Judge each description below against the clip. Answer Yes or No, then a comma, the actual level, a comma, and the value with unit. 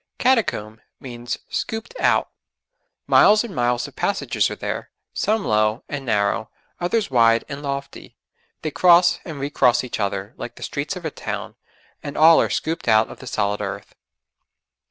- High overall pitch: No, low, 135 Hz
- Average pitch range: No, wide, 7.3 semitones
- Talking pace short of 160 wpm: No, average, 165 wpm